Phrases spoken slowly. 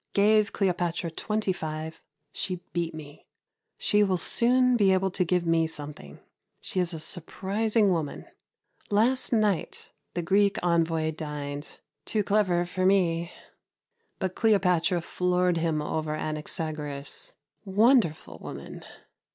Yes: slow, 120 wpm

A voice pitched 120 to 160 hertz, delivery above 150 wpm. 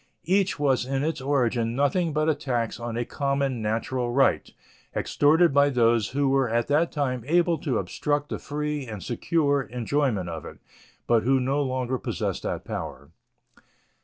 Yes: low, 135 Hz; average, 165 wpm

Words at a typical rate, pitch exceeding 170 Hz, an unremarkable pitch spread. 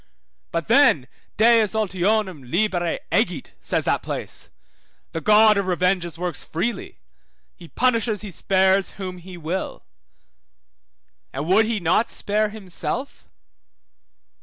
No: slow, 115 wpm; high, 190 Hz; average, 3.7 semitones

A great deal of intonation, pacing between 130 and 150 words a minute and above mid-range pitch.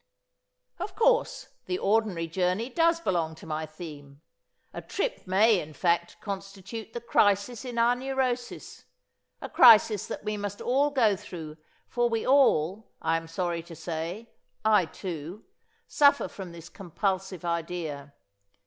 Yes: wide, 5.9 semitones; average, 140 wpm; high, 195 Hz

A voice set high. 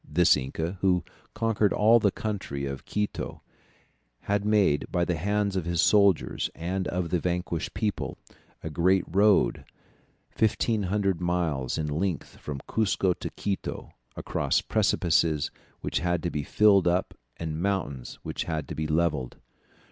No: very low, 90 Hz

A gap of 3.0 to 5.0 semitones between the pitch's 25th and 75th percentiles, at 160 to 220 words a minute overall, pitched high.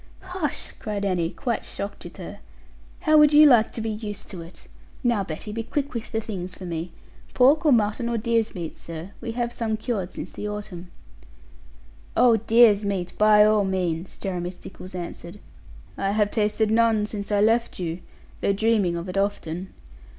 Yes: average, 3.7 semitones; average, 180 wpm; high, 210 Hz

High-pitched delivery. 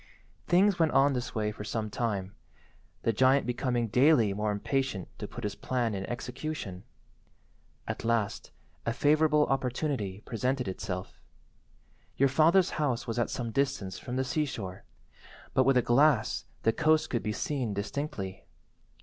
No: low, 125 Hz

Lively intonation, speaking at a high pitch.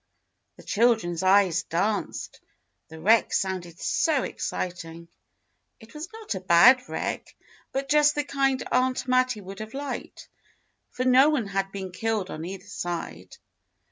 Yes: wide, 5.9 semitones; high, 210 Hz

